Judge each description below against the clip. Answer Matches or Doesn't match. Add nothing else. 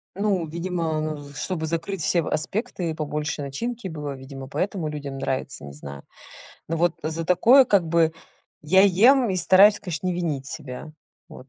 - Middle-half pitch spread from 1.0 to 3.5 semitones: Doesn't match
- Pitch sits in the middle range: Matches